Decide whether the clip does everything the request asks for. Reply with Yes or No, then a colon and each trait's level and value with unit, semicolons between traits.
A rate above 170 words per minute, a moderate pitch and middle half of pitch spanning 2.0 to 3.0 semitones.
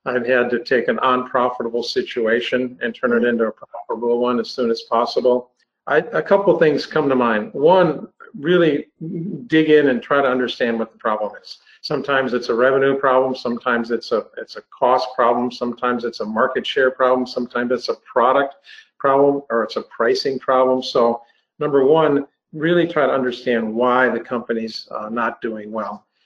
No: average, 185 wpm; low, 125 Hz; average, 2.7 semitones